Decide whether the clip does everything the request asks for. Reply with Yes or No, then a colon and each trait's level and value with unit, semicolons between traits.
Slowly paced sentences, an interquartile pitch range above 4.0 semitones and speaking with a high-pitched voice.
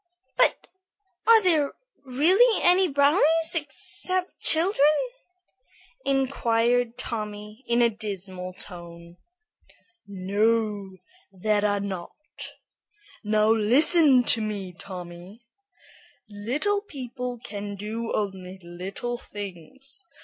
Yes: slow, 90 wpm; wide, 5.5 semitones; high, 225 Hz